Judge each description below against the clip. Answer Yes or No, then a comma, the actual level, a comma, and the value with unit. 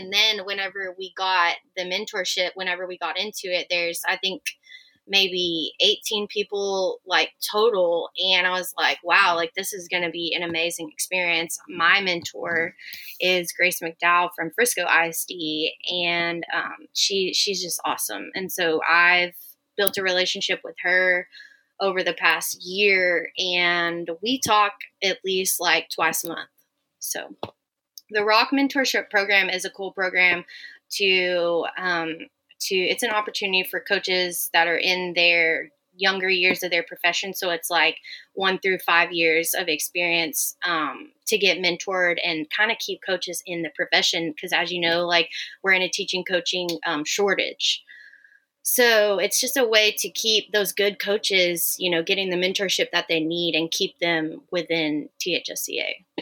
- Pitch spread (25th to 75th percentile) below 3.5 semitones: Yes, average, 2.8 semitones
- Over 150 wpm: Yes, average, 160 wpm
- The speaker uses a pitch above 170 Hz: Yes, medium, 185 Hz